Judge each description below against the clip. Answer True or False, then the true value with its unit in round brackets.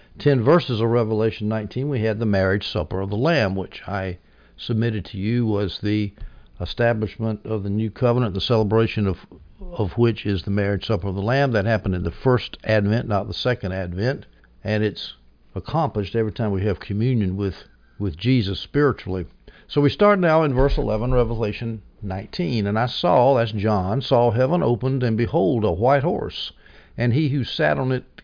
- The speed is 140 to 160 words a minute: False (185 wpm)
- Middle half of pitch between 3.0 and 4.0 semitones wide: True (3.7 semitones)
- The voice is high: False (110 Hz)